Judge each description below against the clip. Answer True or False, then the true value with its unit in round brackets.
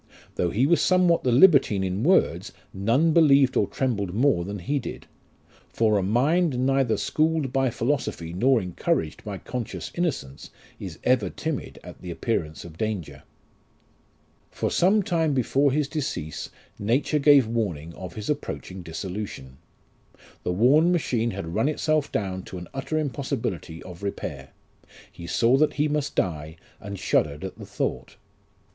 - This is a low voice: True (120 Hz)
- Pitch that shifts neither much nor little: False (7.8 semitones)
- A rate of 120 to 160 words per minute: True (150 wpm)